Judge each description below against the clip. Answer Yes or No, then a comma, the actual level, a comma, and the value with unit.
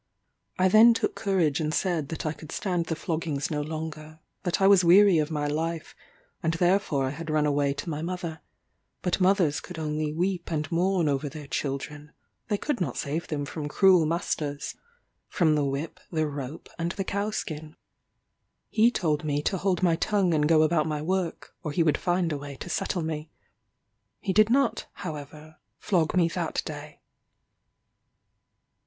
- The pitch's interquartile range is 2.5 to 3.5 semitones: Yes, average, 3.2 semitones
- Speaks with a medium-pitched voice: Yes, medium, 160 Hz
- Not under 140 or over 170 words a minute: No, average, 180 wpm